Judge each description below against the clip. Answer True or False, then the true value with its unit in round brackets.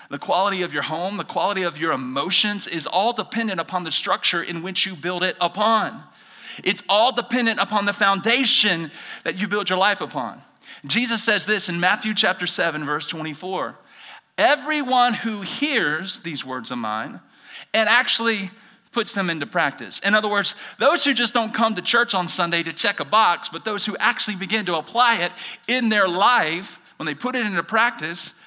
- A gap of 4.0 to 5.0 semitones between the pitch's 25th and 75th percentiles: True (4.7 semitones)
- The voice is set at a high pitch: True (205 Hz)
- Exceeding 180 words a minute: True (190 wpm)